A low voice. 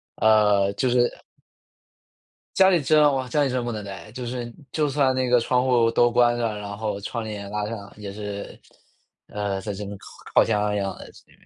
Yes: low, 110 Hz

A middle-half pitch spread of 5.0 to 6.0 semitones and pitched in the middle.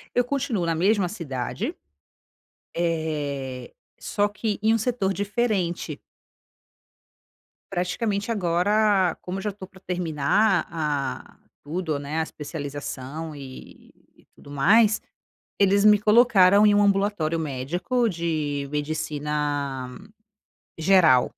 Yes: wide, 5.6 semitones; medium, 175 Hz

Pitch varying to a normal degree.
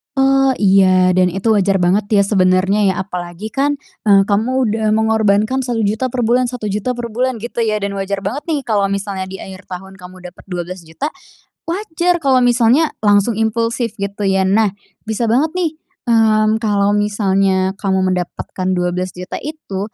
Yes: average, 3.8 semitones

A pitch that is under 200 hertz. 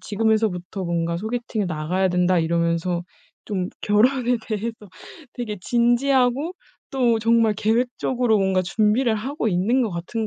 No: high, 215 Hz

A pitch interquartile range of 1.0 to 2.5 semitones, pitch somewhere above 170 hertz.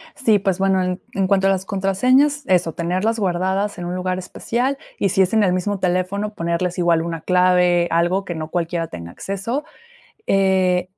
Yes: narrow, 2.0 semitones; medium, 185 Hz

